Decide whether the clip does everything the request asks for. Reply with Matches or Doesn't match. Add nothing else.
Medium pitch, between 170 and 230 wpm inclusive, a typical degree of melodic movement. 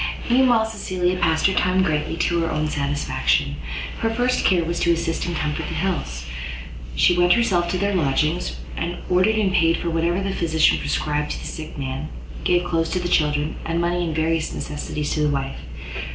Matches